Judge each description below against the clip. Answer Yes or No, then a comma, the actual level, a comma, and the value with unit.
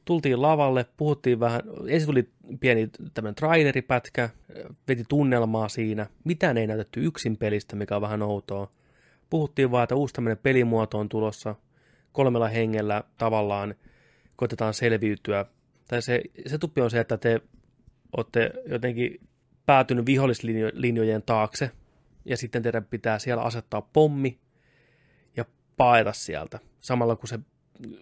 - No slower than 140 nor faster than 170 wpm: No, average, 130 wpm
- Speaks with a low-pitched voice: Yes, low, 120 Hz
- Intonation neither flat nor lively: Yes, average, 3.0 semitones